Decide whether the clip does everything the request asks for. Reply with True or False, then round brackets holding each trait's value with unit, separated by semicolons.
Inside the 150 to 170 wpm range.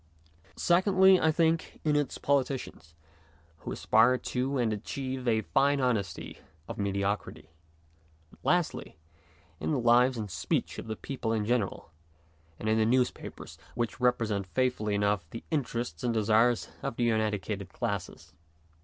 False (140 wpm)